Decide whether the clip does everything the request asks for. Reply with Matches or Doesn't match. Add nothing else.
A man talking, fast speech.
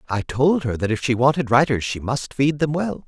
Matches